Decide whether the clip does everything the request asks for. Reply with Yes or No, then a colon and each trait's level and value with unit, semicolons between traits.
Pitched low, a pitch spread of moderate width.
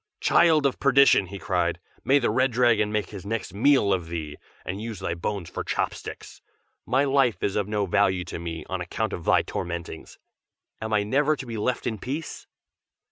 No: low, 105 Hz; wide, 5.8 semitones